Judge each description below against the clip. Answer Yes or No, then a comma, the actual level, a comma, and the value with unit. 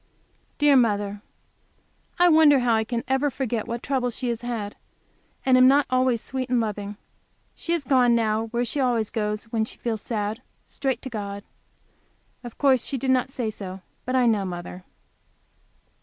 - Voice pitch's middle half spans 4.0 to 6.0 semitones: No, average, 3.3 semitones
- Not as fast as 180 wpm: Yes, average, 170 wpm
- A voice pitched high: Yes, high, 240 Hz